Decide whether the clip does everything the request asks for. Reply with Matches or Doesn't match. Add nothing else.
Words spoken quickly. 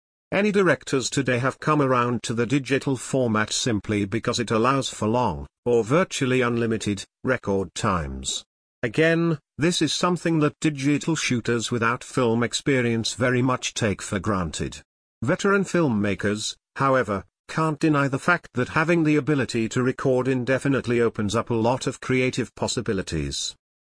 Doesn't match